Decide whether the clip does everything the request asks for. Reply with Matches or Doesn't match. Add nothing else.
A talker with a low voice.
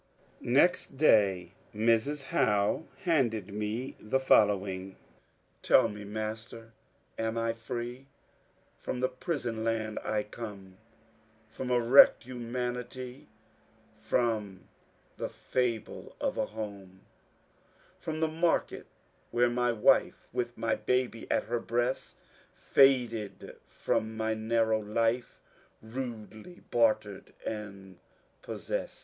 Matches